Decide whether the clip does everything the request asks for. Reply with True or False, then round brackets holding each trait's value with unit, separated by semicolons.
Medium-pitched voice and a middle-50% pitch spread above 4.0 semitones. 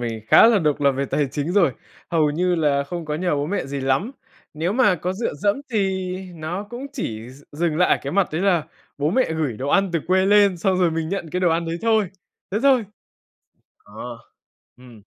True (170 Hz; 5.1 semitones)